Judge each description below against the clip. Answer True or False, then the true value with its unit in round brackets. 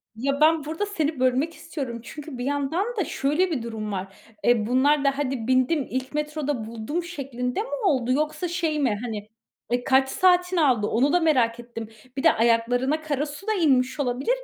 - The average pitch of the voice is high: True (275 Hz)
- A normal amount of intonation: True (4.2 semitones)